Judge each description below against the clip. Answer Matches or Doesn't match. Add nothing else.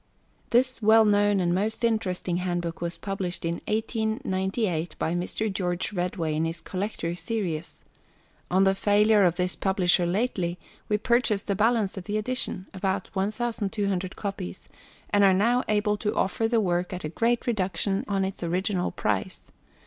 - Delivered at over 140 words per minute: Matches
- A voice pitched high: Matches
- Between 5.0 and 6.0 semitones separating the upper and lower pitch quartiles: Doesn't match